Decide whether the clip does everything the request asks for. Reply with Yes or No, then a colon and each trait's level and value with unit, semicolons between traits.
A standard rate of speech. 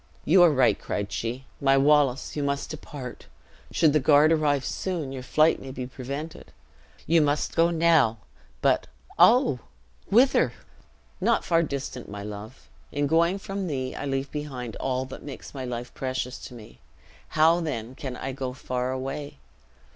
Yes: average, 160 wpm